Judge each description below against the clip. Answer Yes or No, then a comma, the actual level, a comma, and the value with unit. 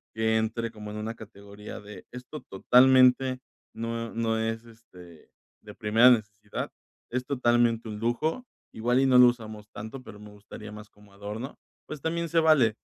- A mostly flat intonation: No, average, 3.0 semitones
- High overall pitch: No, low, 115 Hz